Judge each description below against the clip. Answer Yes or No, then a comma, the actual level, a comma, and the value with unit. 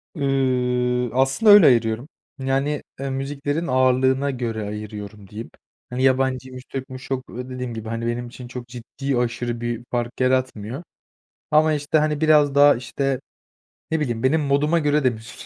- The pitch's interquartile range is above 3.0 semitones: No, average, 2.7 semitones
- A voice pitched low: Yes, low, 130 Hz